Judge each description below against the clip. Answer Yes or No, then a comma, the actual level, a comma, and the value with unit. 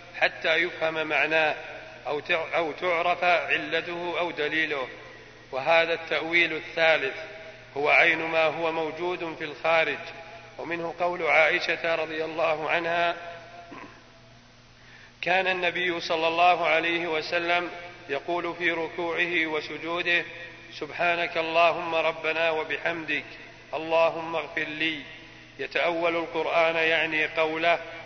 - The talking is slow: No, average, 100 wpm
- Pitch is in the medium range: Yes, medium, 165 Hz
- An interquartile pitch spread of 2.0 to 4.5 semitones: No, narrow, 1.2 semitones